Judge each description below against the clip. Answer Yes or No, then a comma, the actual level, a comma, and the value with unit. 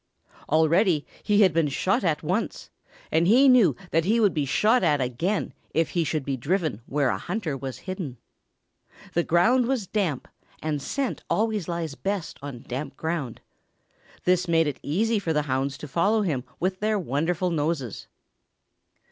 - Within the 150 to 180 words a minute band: Yes, average, 165 wpm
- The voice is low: No, medium, 165 Hz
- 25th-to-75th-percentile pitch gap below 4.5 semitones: No, average, 5.3 semitones